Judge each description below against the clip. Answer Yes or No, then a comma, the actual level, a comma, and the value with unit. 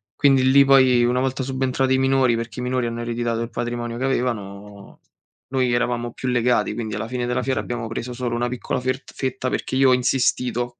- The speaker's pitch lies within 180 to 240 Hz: No, low, 125 Hz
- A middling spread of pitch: No, narrow, 1.7 semitones